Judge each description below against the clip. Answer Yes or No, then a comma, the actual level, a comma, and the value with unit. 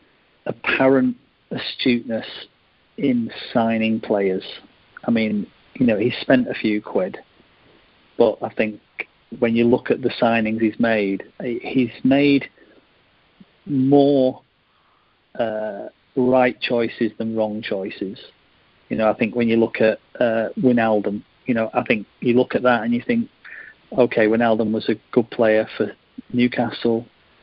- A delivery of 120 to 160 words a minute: Yes, average, 140 wpm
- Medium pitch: No, low, 115 Hz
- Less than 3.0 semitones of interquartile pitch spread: Yes, narrow, 2.5 semitones